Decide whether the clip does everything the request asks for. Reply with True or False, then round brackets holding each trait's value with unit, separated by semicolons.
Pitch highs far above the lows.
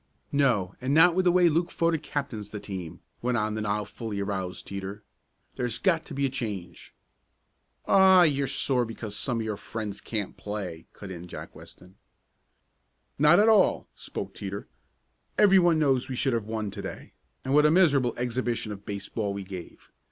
True (6.5 semitones)